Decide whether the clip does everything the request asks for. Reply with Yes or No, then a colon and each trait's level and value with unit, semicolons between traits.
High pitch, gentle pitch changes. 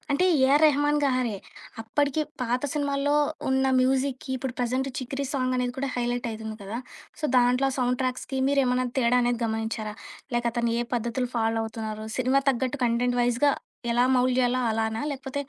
Yes: very high, 250 Hz; narrow, 2.2 semitones